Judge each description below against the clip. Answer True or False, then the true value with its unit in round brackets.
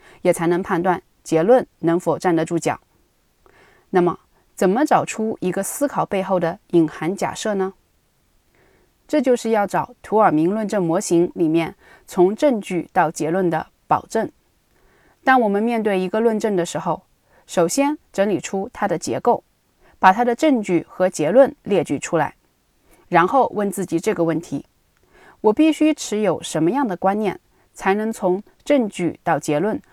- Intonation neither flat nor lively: True (4.6 semitones)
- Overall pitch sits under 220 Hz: True (190 Hz)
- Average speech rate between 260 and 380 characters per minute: False (230 characters per minute)